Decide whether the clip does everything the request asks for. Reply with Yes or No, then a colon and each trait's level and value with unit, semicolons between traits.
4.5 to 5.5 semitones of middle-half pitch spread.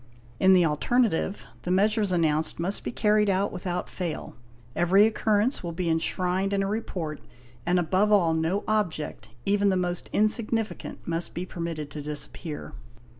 No: average, 3.7 semitones